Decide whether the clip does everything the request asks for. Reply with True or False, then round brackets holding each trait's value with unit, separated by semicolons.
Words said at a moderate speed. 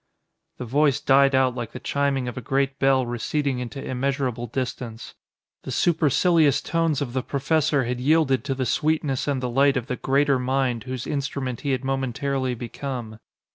True (175 wpm)